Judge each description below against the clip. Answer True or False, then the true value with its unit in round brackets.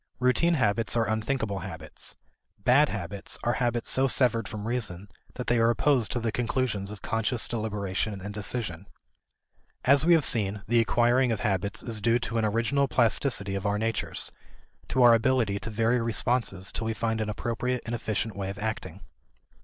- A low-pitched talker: True (115 Hz)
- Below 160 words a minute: False (175 wpm)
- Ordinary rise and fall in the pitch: True (3.0 semitones)